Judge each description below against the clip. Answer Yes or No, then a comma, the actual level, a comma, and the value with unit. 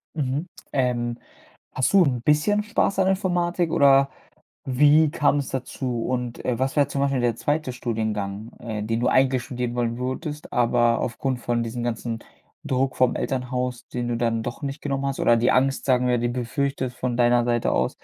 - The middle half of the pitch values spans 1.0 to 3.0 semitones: Yes, average, 2.7 semitones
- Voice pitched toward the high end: No, low, 125 Hz